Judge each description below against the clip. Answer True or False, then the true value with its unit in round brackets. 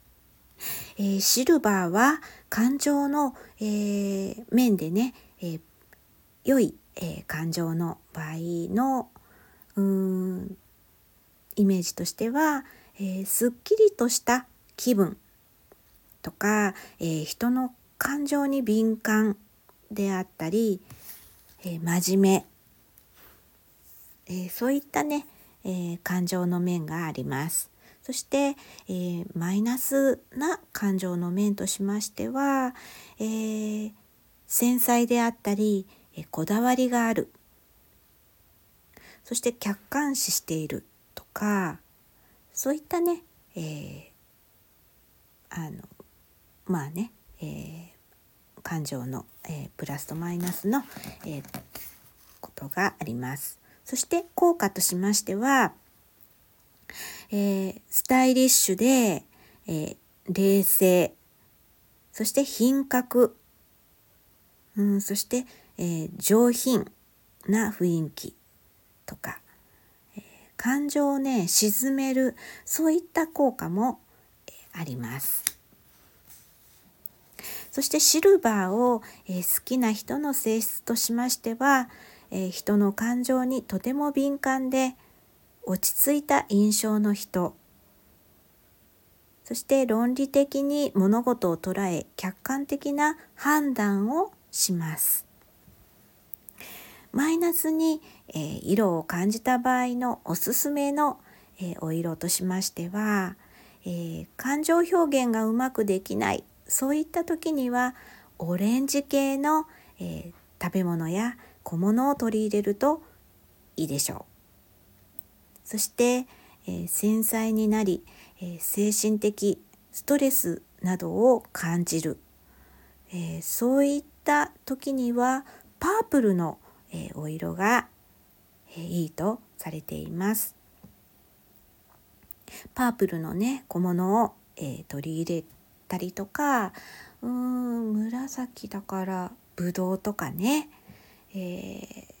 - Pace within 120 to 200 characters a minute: True (195 characters per minute)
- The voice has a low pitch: False (210 Hz)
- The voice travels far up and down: True (6.3 semitones)